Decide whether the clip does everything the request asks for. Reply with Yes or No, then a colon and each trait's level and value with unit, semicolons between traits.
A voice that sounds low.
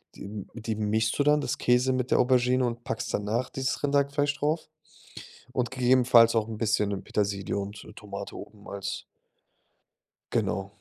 Yes: low, 115 Hz